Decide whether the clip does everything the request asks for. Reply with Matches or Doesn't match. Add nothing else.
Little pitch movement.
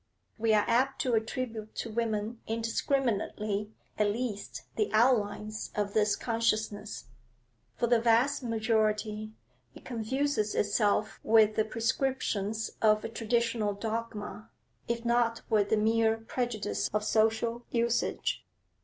Matches